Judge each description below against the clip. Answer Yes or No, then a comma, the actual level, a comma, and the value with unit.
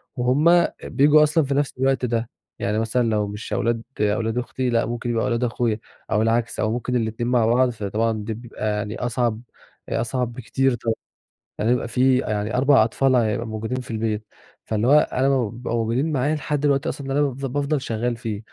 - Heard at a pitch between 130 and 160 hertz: No, low, 120 Hz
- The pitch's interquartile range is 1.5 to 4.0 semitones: Yes, average, 3.0 semitones